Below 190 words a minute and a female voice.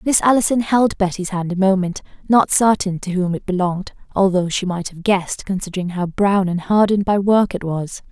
No: average, 200 wpm; female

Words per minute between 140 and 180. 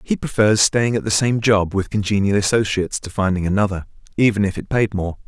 No: fast, 205 wpm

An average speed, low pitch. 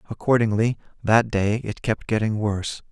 Yes: average, 145 wpm; low, 110 Hz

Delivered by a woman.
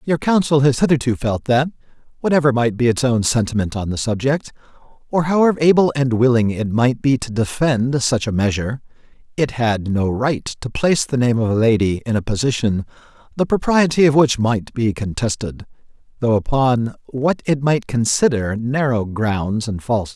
No: male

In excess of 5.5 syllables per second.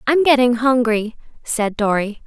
No: 4.4 syllables/s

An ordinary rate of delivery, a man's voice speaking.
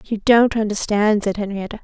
No: average, 165 wpm; female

